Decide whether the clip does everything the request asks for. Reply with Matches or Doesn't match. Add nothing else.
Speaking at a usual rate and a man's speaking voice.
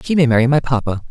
Doesn't match